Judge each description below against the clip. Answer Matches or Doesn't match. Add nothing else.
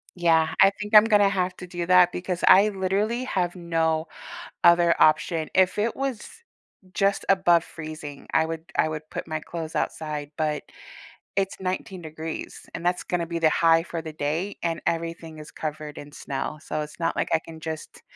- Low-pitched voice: Doesn't match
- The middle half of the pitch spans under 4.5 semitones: Matches